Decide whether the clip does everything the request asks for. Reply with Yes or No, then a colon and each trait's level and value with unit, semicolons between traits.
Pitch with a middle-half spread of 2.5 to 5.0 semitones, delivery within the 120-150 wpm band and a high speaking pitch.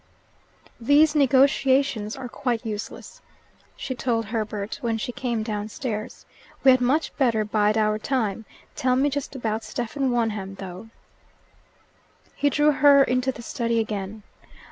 Yes: average, 3.8 semitones; slow, 135 wpm; high, 235 Hz